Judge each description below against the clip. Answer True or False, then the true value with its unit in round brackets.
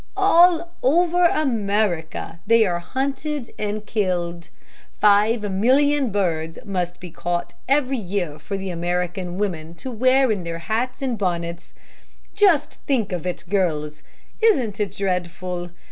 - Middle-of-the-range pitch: False (200 Hz)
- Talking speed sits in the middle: False (130 wpm)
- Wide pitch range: True (6.7 semitones)